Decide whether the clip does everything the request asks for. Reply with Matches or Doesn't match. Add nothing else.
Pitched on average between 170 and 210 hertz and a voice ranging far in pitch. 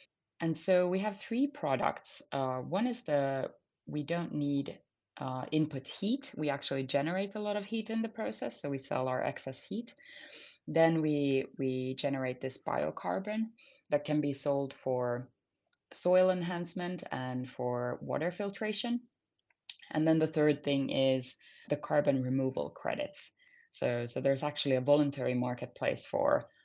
Doesn't match